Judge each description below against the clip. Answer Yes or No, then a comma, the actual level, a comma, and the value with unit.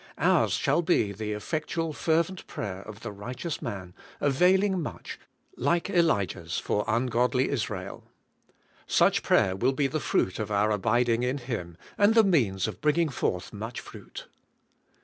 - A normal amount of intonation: No, wide, 7.5 semitones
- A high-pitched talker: No, low, 125 Hz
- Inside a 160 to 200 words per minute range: No, average, 150 wpm